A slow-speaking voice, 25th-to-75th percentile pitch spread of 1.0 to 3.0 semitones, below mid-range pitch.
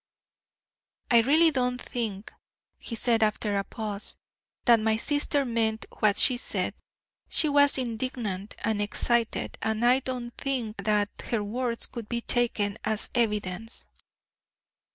No: slow, 130 wpm; average, 2.7 semitones; high, 230 Hz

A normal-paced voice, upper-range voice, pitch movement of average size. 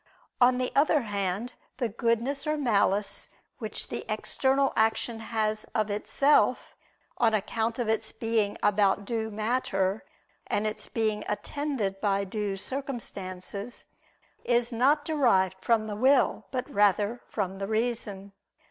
No: slow, 130 wpm; high, 220 Hz; average, 3.4 semitones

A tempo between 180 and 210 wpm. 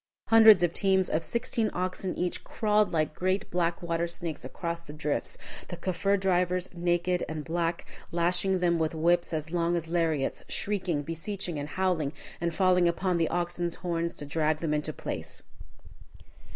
No: average, 165 wpm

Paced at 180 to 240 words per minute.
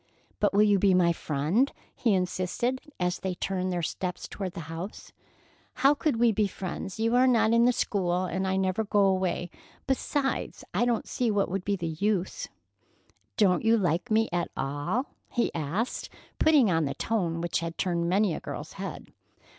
Yes: average, 185 wpm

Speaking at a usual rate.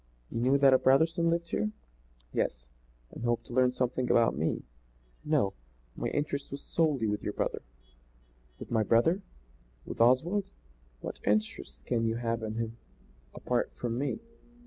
Yes: average, 155 wpm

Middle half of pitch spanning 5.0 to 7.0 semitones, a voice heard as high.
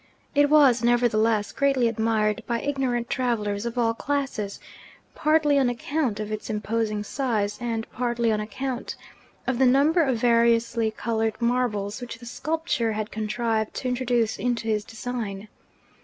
No: narrow, 2.6 semitones; high, 235 Hz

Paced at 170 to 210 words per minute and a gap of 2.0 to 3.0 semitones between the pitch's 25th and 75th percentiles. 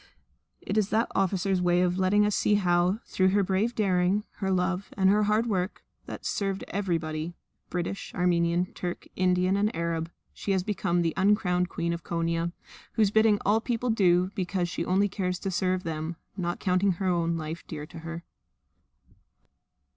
Yes: average, 175 wpm; narrow, 2.6 semitones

